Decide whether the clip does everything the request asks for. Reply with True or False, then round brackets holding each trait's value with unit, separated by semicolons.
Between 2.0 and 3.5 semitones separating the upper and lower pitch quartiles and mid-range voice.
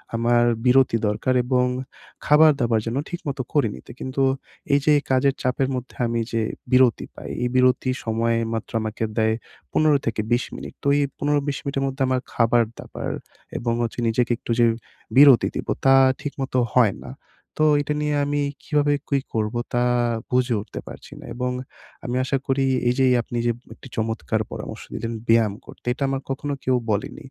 False (3.0 semitones; 125 Hz)